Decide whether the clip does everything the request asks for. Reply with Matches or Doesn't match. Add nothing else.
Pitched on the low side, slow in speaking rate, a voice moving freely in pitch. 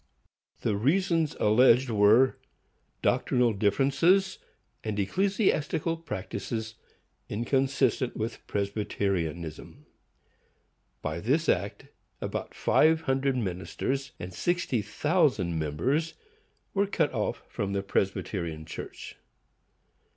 Matches